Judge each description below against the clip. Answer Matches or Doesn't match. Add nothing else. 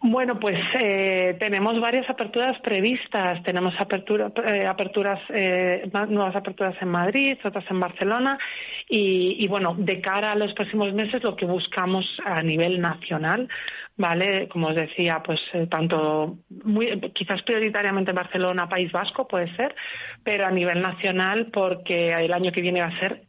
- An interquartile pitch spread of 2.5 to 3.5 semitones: Matches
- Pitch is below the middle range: Doesn't match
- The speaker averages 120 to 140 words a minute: Doesn't match